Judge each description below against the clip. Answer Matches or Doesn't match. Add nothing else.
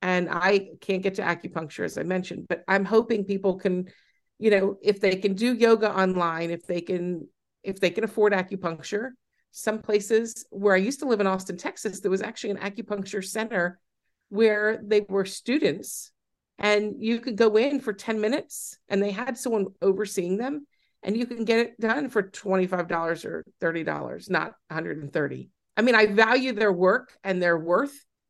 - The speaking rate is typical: Matches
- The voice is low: Doesn't match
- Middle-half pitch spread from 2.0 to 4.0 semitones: Matches